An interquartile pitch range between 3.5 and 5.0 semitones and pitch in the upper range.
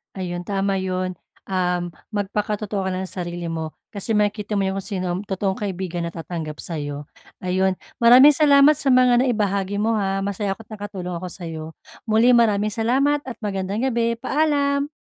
Yes: average, 3.9 semitones; high, 200 Hz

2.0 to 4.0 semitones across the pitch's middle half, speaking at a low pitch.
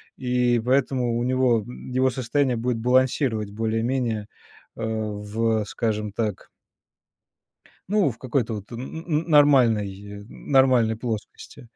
Yes: average, 2.9 semitones; low, 120 Hz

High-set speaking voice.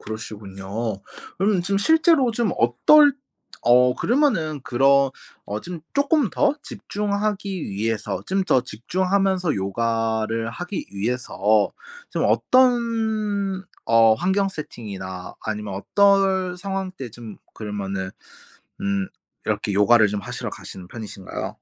No: low, 135 Hz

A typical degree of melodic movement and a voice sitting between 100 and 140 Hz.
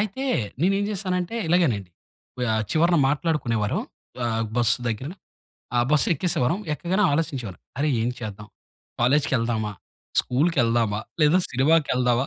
No: wide, 6.6 semitones; low, 135 Hz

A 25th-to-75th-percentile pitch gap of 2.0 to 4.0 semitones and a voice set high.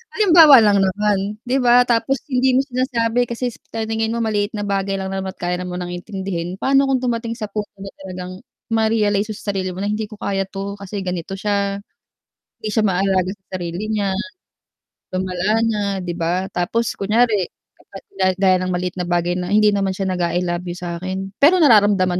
Yes: average, 3.3 semitones; high, 200 Hz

